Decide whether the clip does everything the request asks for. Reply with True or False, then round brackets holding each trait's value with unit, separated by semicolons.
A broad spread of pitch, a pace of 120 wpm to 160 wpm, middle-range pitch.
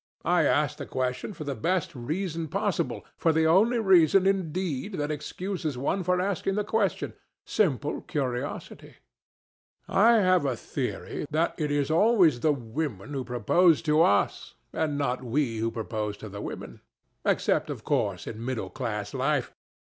True (6.4 semitones; 155 wpm; 150 Hz)